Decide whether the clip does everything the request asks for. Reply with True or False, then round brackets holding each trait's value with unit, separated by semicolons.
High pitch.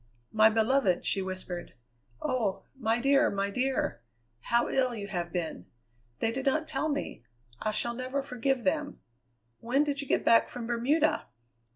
True (240 Hz)